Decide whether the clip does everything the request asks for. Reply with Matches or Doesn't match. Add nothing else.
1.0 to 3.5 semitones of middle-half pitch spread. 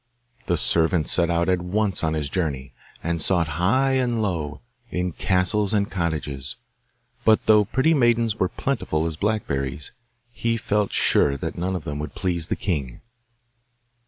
Doesn't match